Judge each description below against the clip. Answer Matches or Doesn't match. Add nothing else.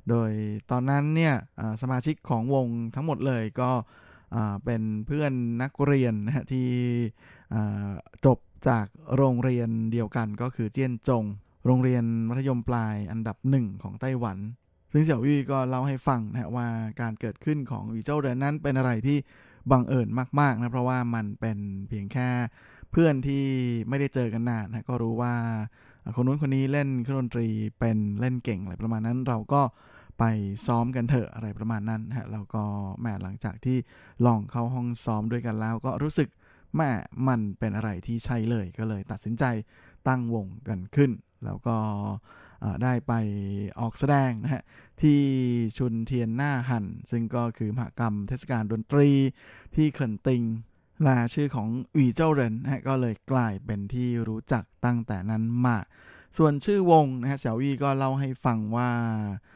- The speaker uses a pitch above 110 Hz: Matches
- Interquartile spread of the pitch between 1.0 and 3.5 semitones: Matches